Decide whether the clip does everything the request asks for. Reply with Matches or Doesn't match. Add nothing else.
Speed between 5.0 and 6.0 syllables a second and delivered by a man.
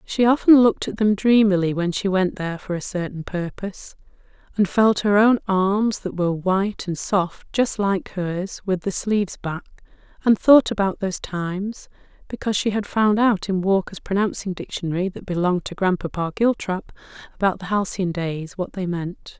Doesn't match